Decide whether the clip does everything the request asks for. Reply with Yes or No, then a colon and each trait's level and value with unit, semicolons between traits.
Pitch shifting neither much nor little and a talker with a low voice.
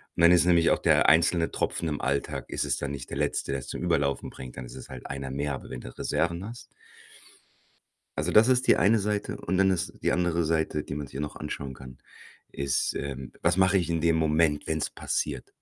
Yes: average, 4.0 semitones; very low, 80 Hz